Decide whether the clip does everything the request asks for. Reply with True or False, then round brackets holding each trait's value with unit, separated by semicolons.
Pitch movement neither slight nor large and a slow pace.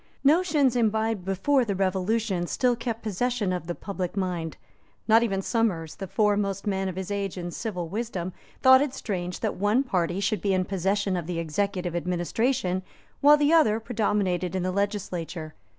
False (3.9 semitones; 170 wpm)